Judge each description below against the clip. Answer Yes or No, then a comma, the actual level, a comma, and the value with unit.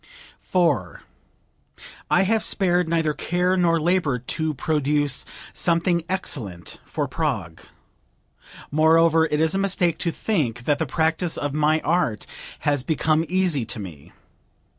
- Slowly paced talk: Yes, slow, 130 wpm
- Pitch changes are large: No, average, 3.6 semitones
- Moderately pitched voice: Yes, medium, 160 Hz